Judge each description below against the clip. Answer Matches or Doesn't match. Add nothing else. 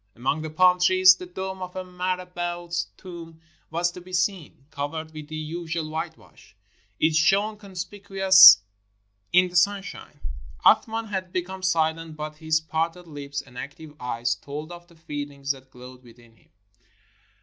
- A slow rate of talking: Doesn't match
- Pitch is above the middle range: Doesn't match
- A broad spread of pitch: Doesn't match